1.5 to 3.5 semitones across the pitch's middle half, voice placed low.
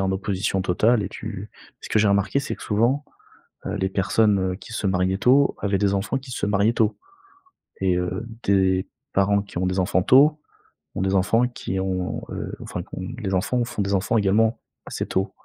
Yes: average, 2.9 semitones; low, 100 Hz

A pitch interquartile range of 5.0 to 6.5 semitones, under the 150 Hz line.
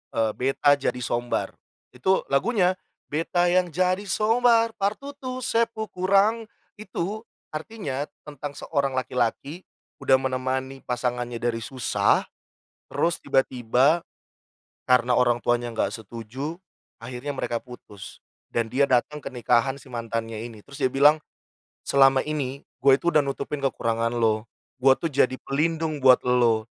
Yes: wide, 5.5 semitones; low, 135 Hz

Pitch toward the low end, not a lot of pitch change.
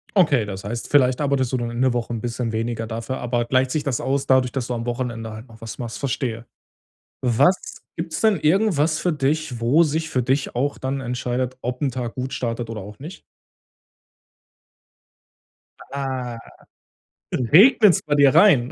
No: low, 130 Hz; average, 3.4 semitones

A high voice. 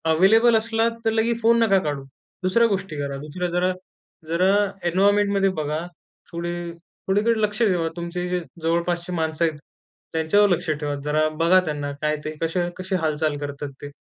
No: medium, 175 Hz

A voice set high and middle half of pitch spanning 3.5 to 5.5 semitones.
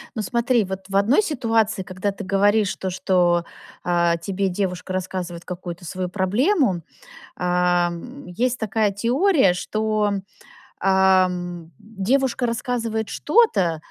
Yes: high, 195 Hz; average, 4.0 semitones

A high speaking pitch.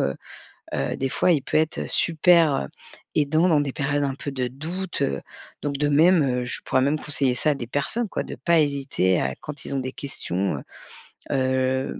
No: medium, 140 Hz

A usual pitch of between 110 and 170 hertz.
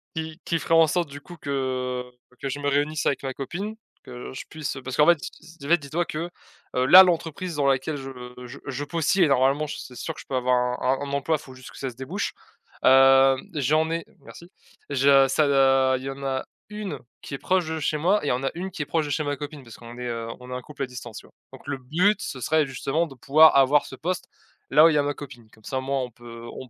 Yes: medium, 140 Hz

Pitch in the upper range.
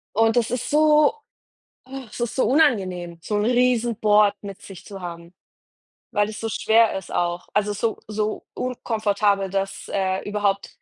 Yes: high, 210 Hz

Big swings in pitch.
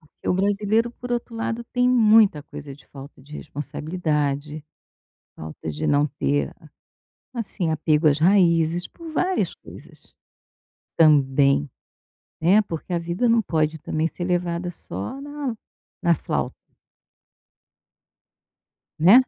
Yes: wide, 6.5 semitones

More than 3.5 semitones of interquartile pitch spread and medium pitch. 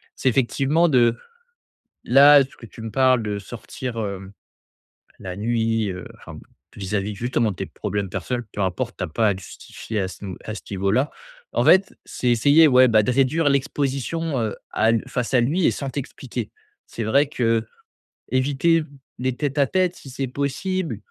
No: average, 4.3 semitones; low, 125 Hz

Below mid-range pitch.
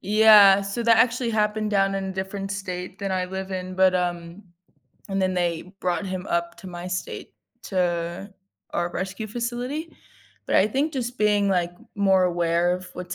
No: high, 190 Hz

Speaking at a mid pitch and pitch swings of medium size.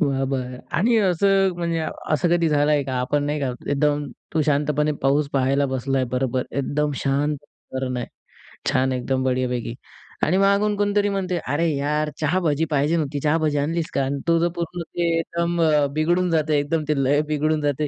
Yes: medium, 150 Hz; average, 3.4 semitones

